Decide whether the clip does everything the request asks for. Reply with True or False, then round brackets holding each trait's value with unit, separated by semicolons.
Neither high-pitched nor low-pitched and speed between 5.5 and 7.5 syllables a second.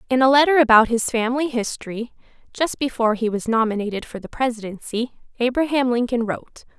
False (240 Hz; 6.1 syllables/s)